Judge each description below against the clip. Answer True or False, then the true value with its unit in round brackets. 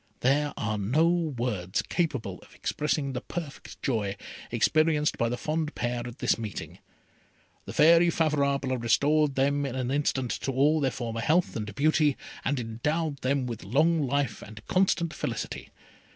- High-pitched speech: False (140 Hz)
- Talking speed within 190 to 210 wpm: False (155 wpm)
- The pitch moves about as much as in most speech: True (4.3 semitones)